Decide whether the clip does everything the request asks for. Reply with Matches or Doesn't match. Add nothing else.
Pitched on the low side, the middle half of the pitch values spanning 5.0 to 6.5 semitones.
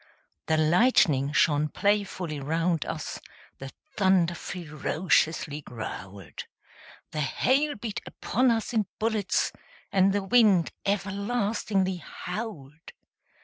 Doesn't match